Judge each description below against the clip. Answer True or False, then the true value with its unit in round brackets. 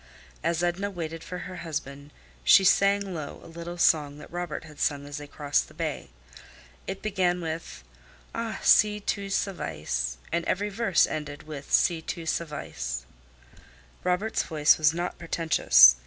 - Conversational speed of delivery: True (155 wpm)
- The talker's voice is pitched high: False (165 Hz)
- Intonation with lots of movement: False (3.7 semitones)